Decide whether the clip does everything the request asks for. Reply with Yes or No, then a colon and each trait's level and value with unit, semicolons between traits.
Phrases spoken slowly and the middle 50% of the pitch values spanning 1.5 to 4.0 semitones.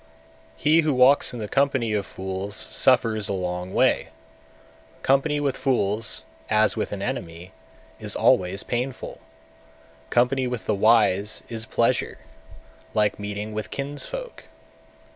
No: slow, 130 wpm; average, 4.8 semitones